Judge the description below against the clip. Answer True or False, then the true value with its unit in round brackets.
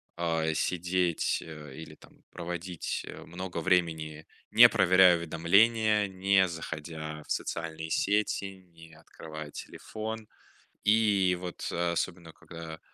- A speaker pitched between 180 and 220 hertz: False (85 Hz)